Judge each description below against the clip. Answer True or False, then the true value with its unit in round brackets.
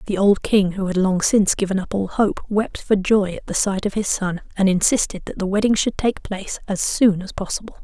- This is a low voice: False (195 Hz)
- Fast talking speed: True (245 wpm)